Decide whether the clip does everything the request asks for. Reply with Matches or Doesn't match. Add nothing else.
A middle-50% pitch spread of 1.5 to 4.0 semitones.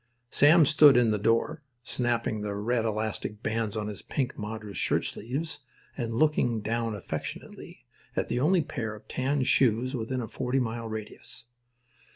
Matches